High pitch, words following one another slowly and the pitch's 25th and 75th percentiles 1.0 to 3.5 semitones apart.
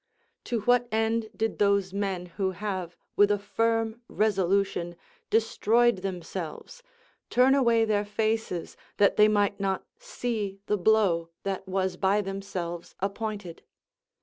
Yes: high, 205 Hz; slow, 125 wpm; average, 2.8 semitones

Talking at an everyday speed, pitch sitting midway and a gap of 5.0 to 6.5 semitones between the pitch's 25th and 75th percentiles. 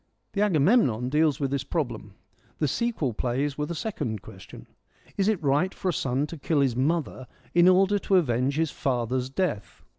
Yes: average, 185 wpm; medium, 145 Hz; wide, 5.6 semitones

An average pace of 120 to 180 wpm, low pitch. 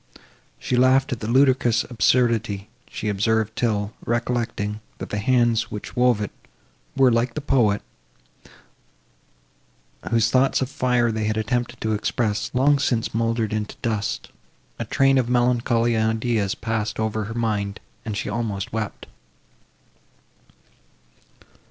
Yes: slow, 135 wpm; low, 115 Hz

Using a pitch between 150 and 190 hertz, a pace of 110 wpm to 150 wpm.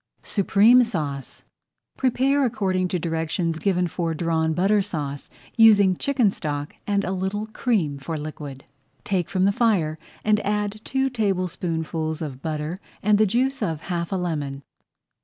Yes: medium, 185 Hz; average, 145 wpm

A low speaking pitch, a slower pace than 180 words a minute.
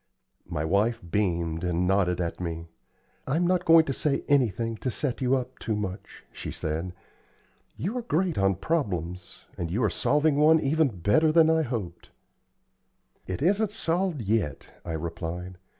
Yes: low, 110 Hz; average, 160 wpm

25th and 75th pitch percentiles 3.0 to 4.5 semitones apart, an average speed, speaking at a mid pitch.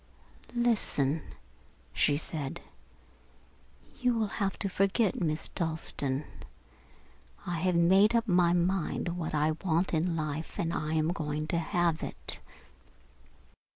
No: average, 3.4 semitones; slow, 120 wpm; medium, 170 Hz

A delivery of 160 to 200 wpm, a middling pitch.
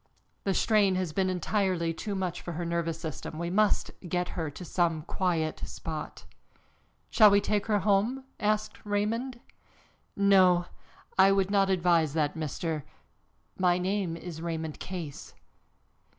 No: average, 145 wpm; medium, 180 Hz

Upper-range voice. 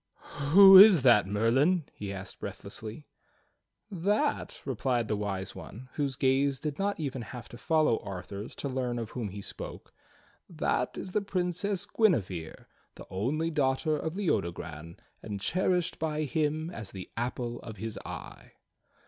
No: low, 130 Hz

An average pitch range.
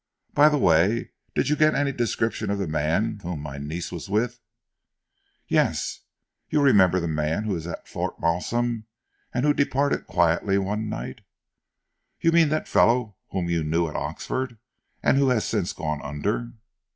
No: wide, 6.7 semitones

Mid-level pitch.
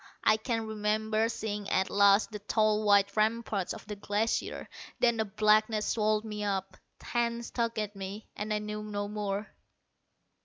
No: high, 215 Hz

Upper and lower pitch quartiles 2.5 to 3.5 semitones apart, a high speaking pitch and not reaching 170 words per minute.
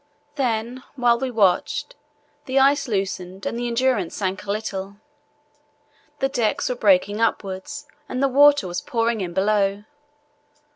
No: average, 4.8 semitones; high, 225 Hz; average, 140 wpm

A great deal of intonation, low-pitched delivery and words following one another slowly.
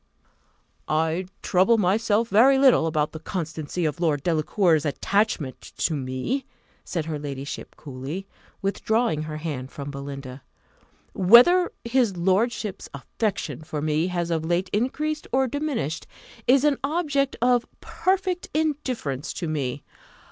No: wide, 7.9 semitones; medium, 180 Hz; slow, 125 wpm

